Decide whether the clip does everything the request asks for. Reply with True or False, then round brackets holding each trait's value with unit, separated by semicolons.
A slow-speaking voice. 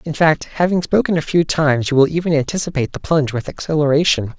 False (205 wpm)